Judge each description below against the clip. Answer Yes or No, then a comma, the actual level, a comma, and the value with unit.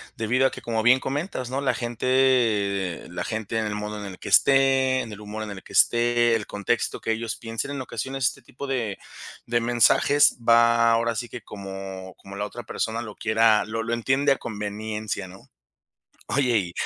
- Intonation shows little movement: No, average, 3.1 semitones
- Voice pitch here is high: No, low, 115 Hz